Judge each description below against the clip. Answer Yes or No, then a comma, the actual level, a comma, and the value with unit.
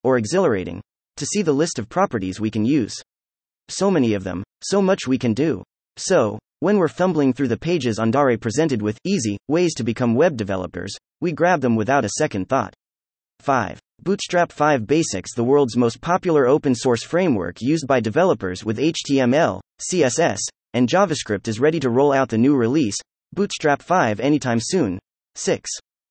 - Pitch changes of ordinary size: No, wide, 6.0 semitones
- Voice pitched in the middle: No, low, 130 Hz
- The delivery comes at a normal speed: Yes, average, 170 wpm